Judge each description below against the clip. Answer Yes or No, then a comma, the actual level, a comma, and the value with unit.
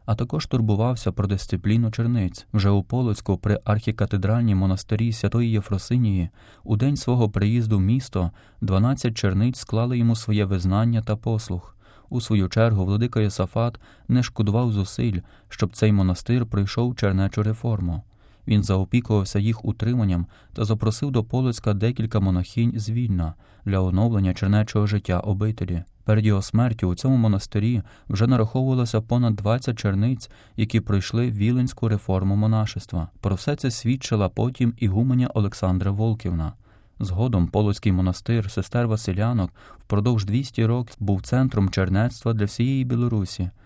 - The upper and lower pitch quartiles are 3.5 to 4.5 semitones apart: No, average, 2.9 semitones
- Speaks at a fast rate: No, average, 135 wpm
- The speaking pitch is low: Yes, low, 110 Hz